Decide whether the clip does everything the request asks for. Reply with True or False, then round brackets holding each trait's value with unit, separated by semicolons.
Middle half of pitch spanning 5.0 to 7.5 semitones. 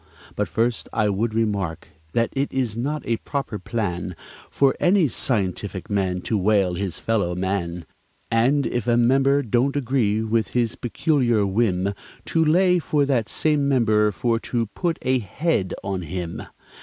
True (5.4 semitones)